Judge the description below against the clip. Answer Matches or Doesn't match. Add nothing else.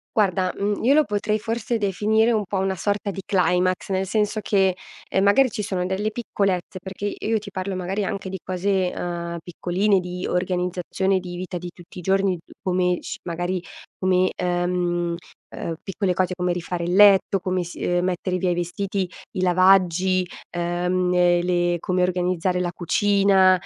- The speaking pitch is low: Doesn't match